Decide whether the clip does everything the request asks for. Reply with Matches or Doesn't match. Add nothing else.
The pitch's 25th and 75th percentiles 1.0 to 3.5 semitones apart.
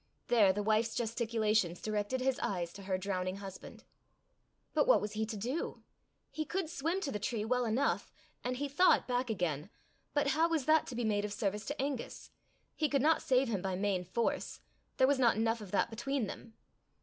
Doesn't match